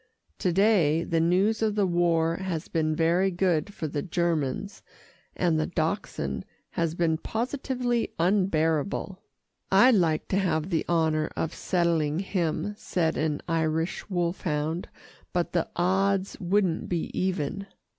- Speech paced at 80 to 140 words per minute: Yes, slow, 135 wpm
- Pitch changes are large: No, average, 3.2 semitones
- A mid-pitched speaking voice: Yes, medium, 175 Hz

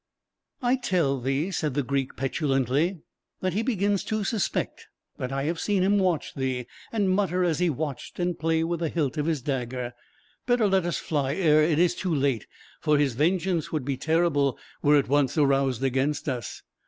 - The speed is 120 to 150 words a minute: No, average, 190 wpm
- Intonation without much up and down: No, average, 4.7 semitones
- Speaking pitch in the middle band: Yes, medium, 155 Hz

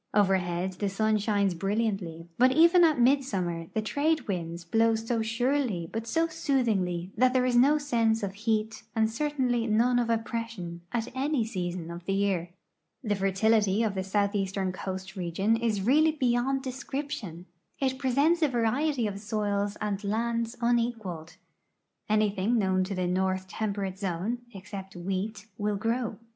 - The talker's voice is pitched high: Yes, high, 215 Hz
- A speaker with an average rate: Yes, average, 150 wpm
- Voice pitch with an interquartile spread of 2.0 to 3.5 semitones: No, average, 4.1 semitones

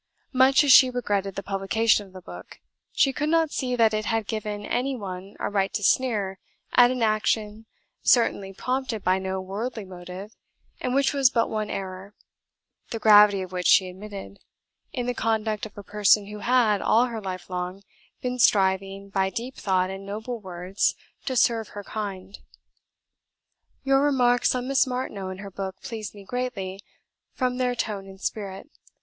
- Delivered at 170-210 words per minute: Yes, average, 175 wpm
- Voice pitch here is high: Yes, high, 210 Hz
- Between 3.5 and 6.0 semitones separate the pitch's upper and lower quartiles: Yes, average, 4.2 semitones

